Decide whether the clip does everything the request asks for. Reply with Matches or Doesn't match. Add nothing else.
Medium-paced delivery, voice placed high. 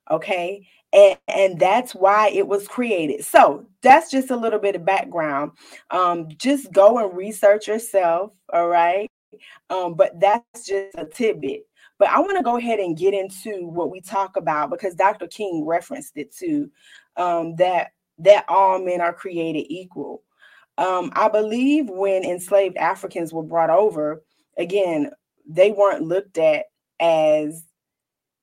Matches